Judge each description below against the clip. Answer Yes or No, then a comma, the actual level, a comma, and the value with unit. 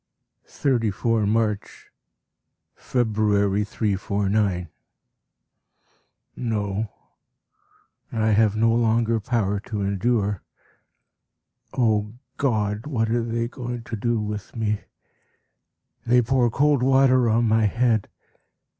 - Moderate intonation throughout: No, narrow, 2.3 semitones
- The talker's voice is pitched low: Yes, low, 110 Hz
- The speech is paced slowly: Yes, slow, 95 wpm